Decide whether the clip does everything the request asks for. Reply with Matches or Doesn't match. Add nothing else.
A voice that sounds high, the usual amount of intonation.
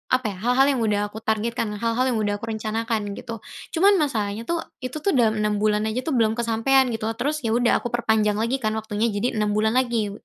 Doesn't match